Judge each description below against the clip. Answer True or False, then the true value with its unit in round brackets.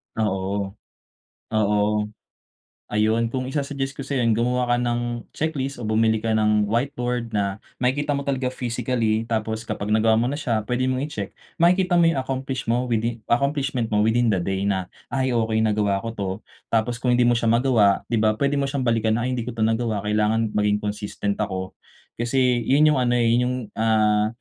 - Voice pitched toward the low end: True (115 Hz)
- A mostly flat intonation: False (3.1 semitones)